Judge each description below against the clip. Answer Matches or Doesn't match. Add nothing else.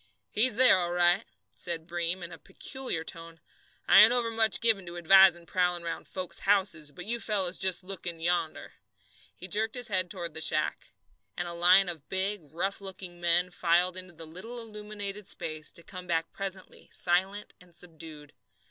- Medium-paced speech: Matches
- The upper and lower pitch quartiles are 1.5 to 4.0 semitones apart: Matches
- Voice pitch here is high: Doesn't match